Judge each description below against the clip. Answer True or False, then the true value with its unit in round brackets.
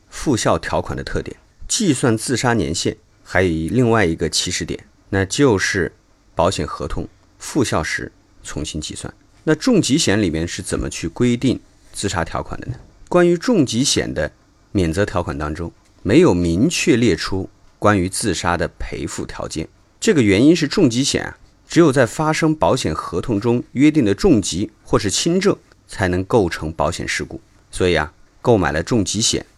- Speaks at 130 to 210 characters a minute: False (255 characters per minute)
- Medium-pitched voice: False (100 Hz)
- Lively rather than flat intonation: True (5.7 semitones)